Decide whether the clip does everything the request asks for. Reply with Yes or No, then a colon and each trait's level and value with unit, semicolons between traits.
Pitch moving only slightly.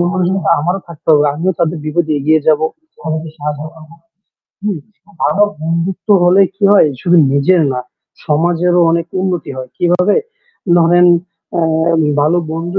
Yes: narrow, 2.3 semitones